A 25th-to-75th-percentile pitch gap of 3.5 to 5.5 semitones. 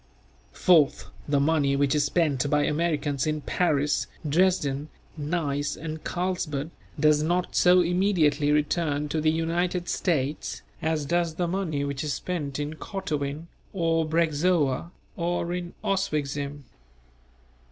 No: average, 3.1 semitones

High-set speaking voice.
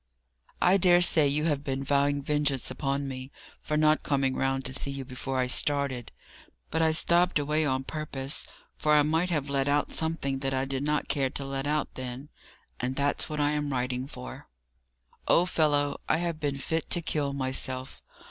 No: medium, 140 Hz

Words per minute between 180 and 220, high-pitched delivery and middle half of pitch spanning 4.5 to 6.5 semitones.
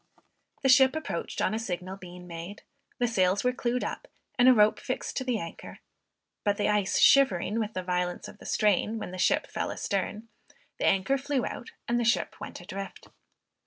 Yes: average, 195 wpm; high, 210 Hz; average, 5.0 semitones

